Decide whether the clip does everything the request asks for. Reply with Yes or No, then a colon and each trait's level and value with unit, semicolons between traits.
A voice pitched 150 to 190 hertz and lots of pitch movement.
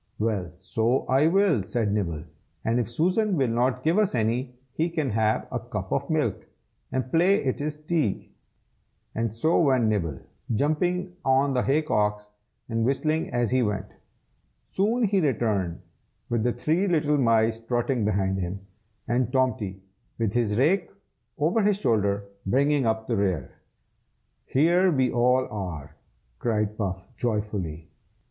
No: low, 120 Hz; wide, 6.3 semitones